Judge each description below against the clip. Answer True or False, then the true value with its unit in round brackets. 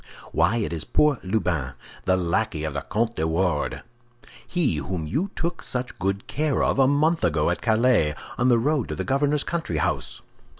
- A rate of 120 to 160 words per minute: False (180 wpm)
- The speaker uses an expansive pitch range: True (8.6 semitones)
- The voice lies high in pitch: False (110 Hz)